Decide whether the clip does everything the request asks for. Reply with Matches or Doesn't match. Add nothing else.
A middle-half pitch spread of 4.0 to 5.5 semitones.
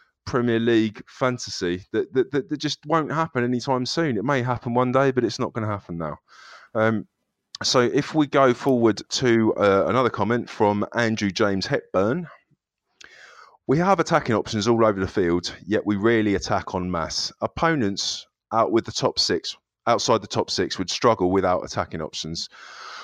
Matches